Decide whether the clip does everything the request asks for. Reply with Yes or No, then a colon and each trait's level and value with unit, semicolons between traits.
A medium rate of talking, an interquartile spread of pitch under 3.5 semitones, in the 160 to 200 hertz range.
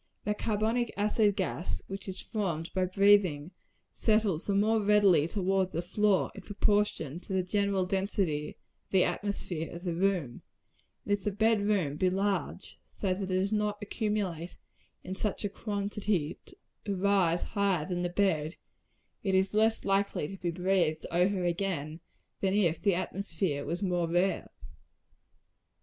Yes: average, 160 wpm; average, 2.7 semitones; high, 190 Hz